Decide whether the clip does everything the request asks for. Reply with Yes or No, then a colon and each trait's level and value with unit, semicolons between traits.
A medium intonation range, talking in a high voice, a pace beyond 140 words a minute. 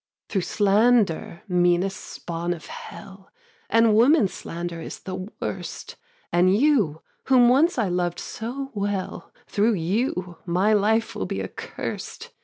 No: average, 4.6 semitones; high, 195 Hz; slow, 135 wpm